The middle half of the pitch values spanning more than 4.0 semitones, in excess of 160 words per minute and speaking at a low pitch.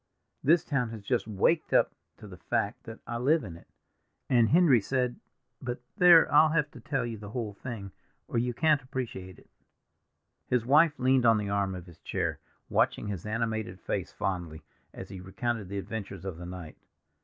Yes: average, 5.0 semitones; average, 185 wpm; low, 115 Hz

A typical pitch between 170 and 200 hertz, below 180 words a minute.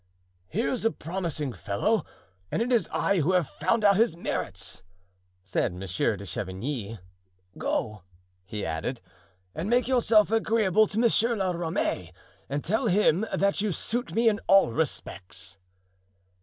Yes: medium, 185 Hz; average, 145 wpm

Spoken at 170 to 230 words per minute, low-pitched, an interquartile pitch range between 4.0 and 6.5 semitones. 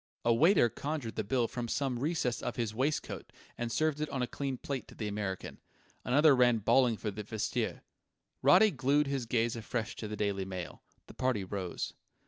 Yes: average, 190 wpm; low, 120 Hz; average, 4.3 semitones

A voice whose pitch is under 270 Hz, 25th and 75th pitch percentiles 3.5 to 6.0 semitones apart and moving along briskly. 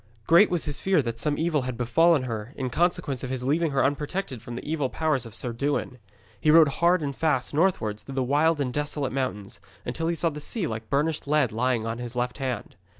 Yes: medium, 140 Hz; average, 4.3 semitones; fast, 225 wpm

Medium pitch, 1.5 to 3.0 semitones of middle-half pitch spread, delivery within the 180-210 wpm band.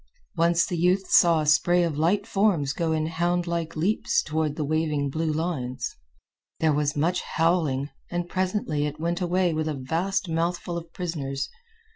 No: medium, 165 Hz; narrow, 2.5 semitones; average, 165 wpm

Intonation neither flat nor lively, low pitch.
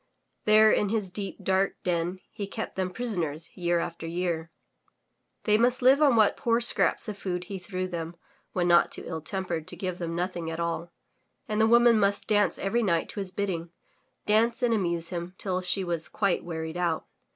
No: average, 3.6 semitones; medium, 185 Hz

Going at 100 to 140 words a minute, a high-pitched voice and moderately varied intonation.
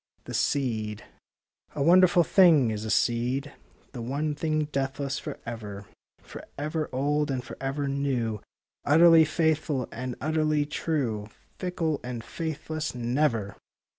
No: slow, 135 wpm; medium, 140 Hz; average, 4.3 semitones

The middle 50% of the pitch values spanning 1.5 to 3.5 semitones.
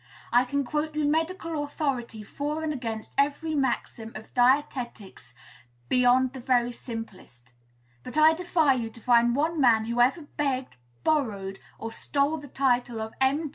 No: average, 4.0 semitones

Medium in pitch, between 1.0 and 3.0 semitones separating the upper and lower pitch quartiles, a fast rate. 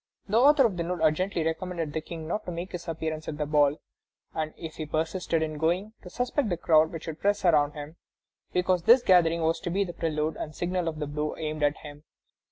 Yes: medium, 165 Hz; average, 2.7 semitones; fast, 230 wpm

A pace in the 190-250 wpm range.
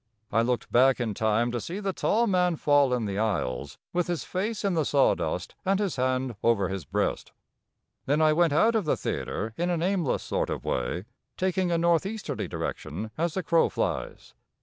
Yes: average, 195 wpm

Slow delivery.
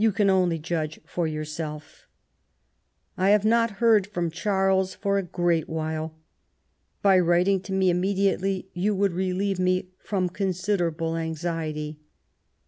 Yes: slow, 130 wpm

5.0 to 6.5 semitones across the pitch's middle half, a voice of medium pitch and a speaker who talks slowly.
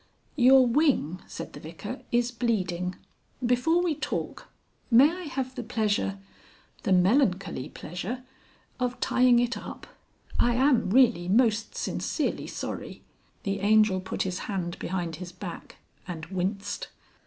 No: wide, 5.4 semitones; high, 220 Hz; slow, 130 wpm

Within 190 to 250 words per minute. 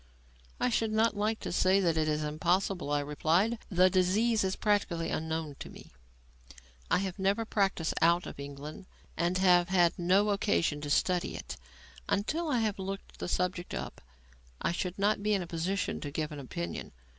No: average, 180 wpm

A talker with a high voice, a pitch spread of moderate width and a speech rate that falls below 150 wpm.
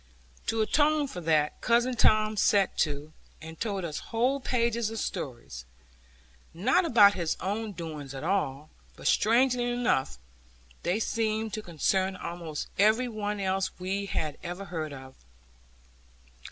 No: high, 200 Hz; wide, 5.7 semitones; average, 140 wpm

